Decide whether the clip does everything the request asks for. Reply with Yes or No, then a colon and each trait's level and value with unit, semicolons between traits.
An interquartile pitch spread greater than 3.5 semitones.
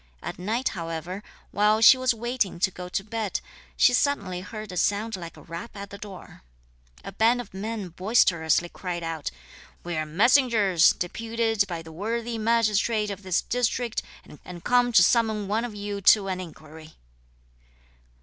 Yes: average, 4.2 semitones